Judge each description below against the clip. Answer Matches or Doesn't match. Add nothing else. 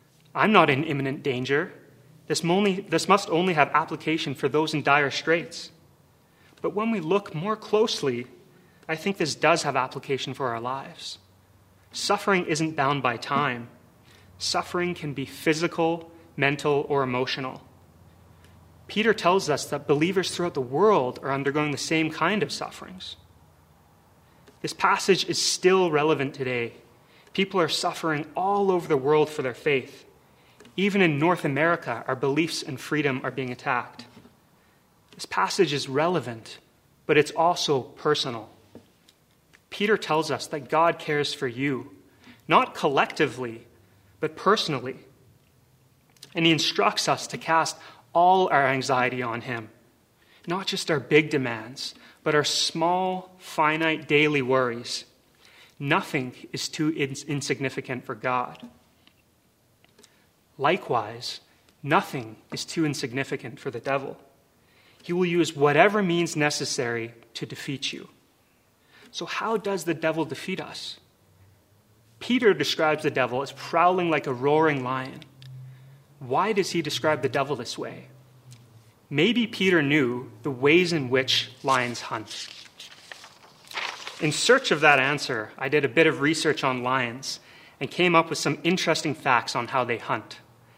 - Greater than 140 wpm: Doesn't match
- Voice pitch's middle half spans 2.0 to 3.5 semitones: Doesn't match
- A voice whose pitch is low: Doesn't match